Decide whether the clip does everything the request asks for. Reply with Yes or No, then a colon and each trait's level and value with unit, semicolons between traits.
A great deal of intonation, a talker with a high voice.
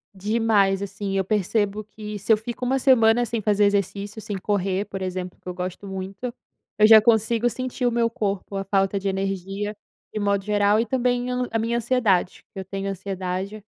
No: narrow, 2.6 semitones; high, 205 Hz